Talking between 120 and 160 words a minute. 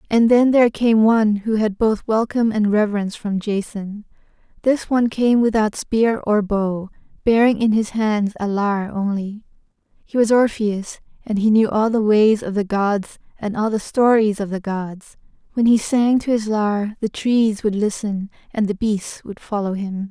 No: average, 185 wpm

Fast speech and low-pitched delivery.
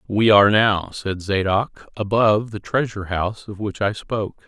No: average, 175 wpm; low, 105 Hz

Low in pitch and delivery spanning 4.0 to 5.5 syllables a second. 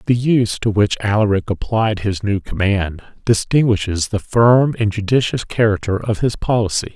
Yes: low, 110 Hz; 4.8 syllables/s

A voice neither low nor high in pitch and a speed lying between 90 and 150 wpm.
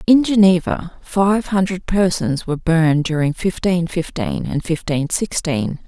Yes: medium, 175 Hz; slow, 135 wpm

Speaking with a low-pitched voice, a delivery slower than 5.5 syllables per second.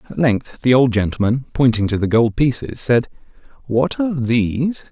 Yes: low, 125 Hz; 5.0 syllables/s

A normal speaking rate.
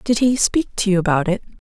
No: fast, 255 wpm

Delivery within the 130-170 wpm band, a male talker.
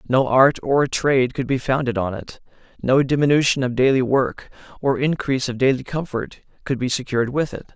No: average, 185 wpm; male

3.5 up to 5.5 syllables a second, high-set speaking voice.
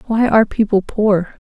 Yes: 4.8 syllables/s; high, 205 Hz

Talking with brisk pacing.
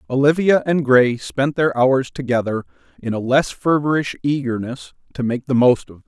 No: average, 180 wpm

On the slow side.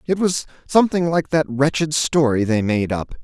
No: average, 185 wpm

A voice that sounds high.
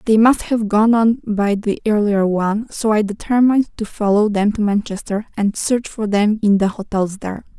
Yes: high, 210 Hz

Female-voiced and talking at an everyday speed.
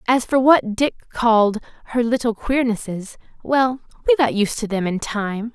Yes: female; average, 160 wpm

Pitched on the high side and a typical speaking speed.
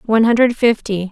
Yes: high, 220 Hz; average, 160 wpm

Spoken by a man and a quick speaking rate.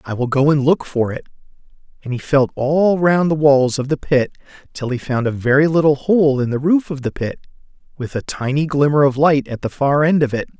Yes: male; fast, 240 wpm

